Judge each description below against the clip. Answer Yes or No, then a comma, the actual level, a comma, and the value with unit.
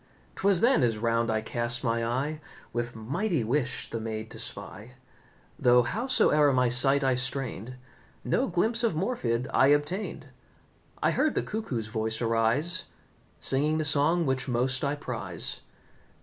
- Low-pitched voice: Yes, low, 130 Hz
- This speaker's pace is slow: No, average, 150 wpm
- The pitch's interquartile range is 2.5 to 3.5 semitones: No, average, 4.9 semitones